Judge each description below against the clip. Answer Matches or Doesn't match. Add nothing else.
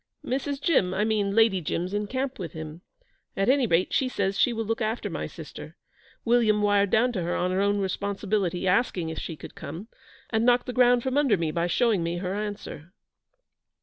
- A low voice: Doesn't match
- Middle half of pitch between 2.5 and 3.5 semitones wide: Doesn't match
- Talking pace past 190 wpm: Matches